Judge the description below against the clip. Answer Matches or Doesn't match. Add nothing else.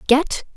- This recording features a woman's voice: Matches